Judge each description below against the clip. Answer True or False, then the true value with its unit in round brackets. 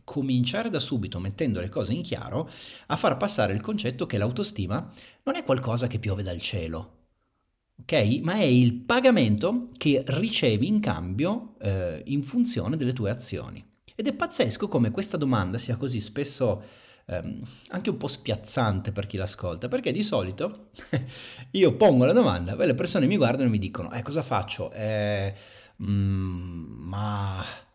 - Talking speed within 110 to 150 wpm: False (160 wpm)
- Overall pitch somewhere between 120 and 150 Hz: False (110 Hz)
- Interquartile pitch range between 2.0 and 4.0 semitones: False (4.8 semitones)